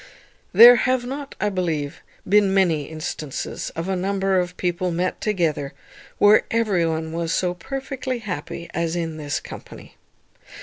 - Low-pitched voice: No, medium, 180 Hz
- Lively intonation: No, average, 4.1 semitones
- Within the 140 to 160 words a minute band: Yes, average, 145 wpm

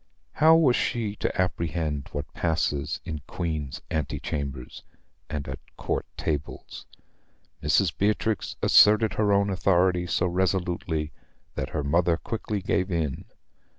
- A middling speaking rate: No, slow, 125 wpm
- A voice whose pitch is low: Yes, very low, 85 Hz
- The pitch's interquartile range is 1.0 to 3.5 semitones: No, average, 4.8 semitones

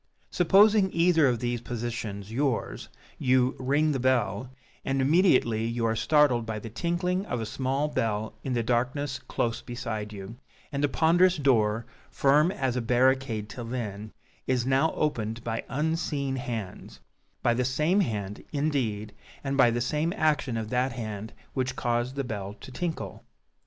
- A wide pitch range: No, average, 4.2 semitones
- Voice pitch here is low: Yes, low, 125 Hz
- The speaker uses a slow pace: No, average, 160 wpm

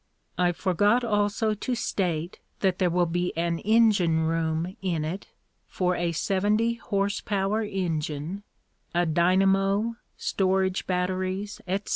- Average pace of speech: No, slow, 125 wpm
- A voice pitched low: No, medium, 185 Hz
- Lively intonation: No, average, 2.9 semitones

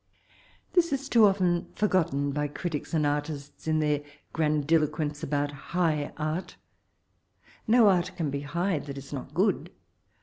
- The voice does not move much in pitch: No, average, 3.7 semitones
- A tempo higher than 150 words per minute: No, average, 140 wpm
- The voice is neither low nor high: Yes, medium, 155 Hz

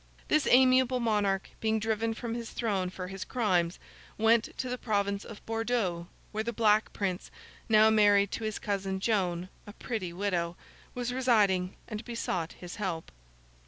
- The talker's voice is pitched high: Yes, high, 210 Hz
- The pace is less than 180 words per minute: Yes, average, 150 wpm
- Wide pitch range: No, average, 3.3 semitones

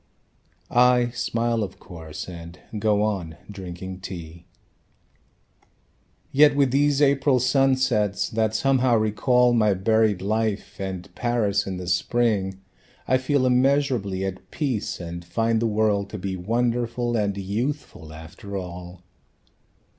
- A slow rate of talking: Yes, slow, 125 wpm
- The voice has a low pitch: Yes, low, 110 Hz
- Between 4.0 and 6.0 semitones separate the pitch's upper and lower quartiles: Yes, average, 4.6 semitones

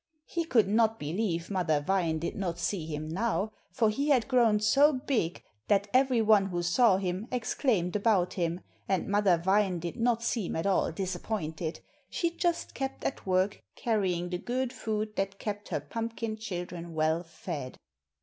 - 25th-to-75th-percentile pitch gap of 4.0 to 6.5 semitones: Yes, average, 4.7 semitones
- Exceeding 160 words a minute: Yes, average, 170 wpm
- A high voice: Yes, high, 200 Hz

